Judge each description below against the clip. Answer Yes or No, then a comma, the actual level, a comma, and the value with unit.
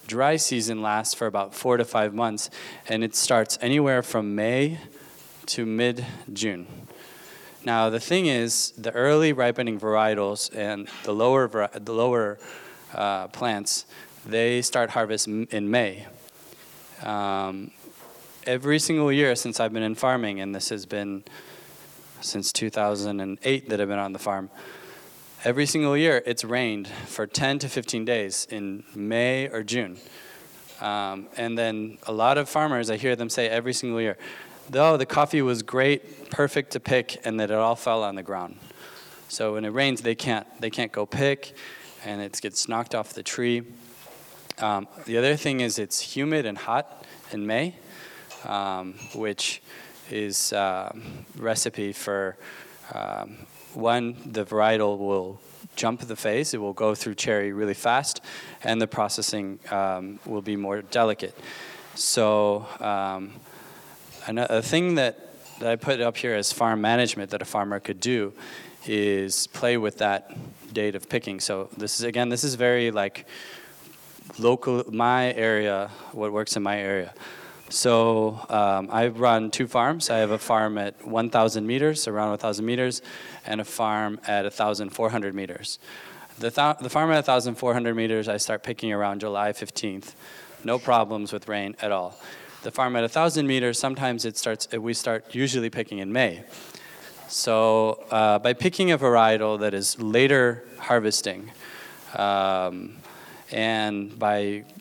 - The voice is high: No, low, 110 Hz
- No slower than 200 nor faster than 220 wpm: No, average, 155 wpm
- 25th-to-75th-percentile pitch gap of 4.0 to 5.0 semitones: No, average, 2.9 semitones